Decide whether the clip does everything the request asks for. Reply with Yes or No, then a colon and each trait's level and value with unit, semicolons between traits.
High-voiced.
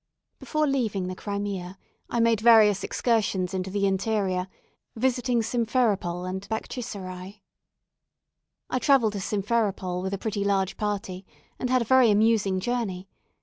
Yes: high, 205 Hz